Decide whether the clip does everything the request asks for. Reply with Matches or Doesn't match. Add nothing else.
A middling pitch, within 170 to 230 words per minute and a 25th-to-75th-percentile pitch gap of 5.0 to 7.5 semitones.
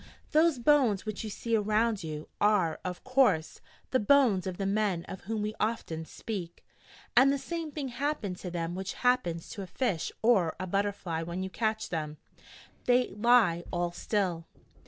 Doesn't match